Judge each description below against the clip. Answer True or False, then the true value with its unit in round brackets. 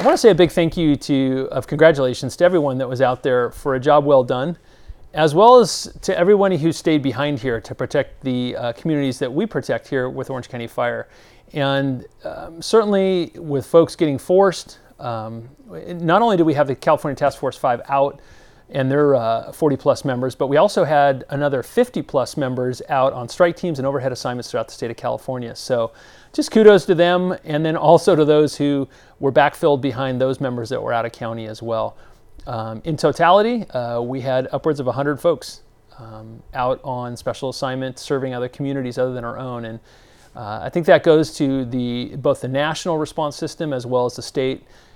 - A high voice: False (140 Hz)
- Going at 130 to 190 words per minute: False (205 wpm)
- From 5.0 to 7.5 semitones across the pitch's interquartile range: False (4.0 semitones)